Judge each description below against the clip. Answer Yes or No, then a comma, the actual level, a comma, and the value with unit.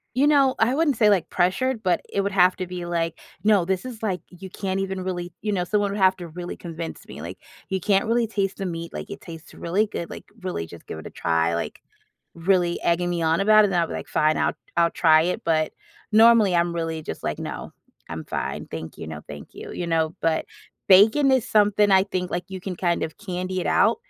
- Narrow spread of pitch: No, average, 3.4 semitones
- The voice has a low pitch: No, medium, 180 Hz